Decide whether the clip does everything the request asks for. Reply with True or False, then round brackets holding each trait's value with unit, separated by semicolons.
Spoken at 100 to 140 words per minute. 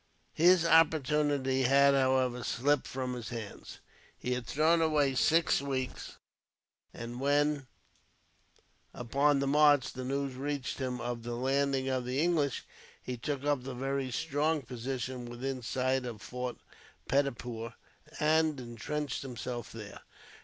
True (135 wpm)